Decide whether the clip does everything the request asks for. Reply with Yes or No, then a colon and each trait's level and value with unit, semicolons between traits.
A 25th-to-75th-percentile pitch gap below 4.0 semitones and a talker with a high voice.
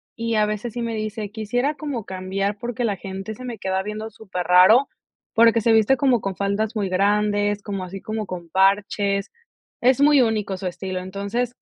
Yes: average, 2.8 semitones; high, 210 Hz